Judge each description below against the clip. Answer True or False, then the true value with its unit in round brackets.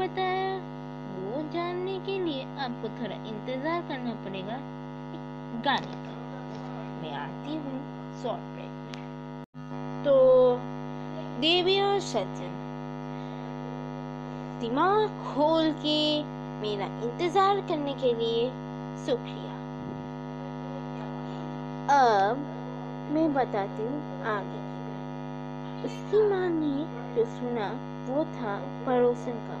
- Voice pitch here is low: False (300 Hz)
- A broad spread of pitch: True (7.0 semitones)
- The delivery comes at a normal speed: False (75 wpm)